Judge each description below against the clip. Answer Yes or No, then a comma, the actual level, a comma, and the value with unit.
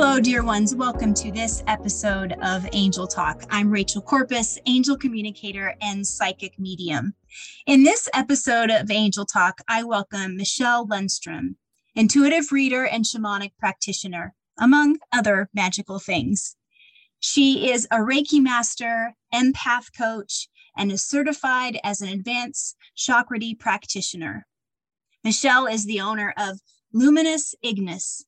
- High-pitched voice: Yes, high, 220 Hz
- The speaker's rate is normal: No, slow, 125 wpm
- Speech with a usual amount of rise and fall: Yes, average, 4.2 semitones